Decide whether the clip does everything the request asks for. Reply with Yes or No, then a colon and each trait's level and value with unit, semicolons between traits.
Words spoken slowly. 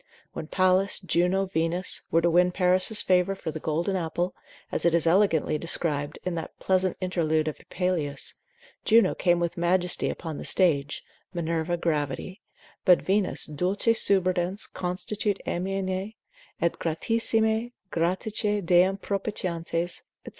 Yes: slow, 130 wpm